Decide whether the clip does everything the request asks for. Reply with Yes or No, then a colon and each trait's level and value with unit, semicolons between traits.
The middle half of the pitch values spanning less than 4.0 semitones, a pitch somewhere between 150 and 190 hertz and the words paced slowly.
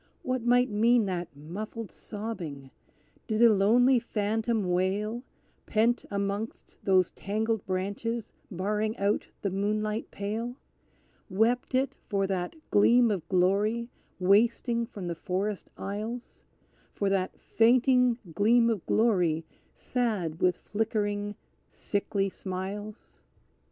No: average, 3.1 semitones; high, 210 Hz; slow, 110 wpm